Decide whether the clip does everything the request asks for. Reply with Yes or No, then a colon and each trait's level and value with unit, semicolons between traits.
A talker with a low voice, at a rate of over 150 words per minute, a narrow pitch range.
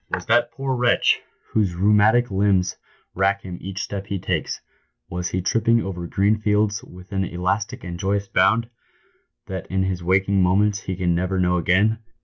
Yes: very low, 95 Hz; average, 175 wpm; narrow, 2.3 semitones